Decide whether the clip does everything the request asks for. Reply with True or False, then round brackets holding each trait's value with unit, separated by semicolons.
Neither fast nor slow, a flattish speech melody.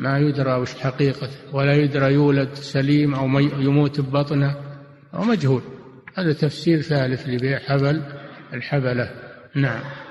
True (120 wpm; 1.4 semitones)